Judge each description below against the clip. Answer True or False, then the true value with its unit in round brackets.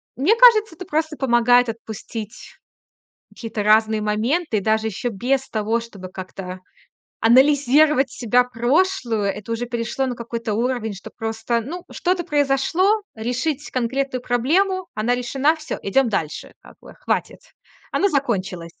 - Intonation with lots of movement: False (4.7 semitones)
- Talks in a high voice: True (245 Hz)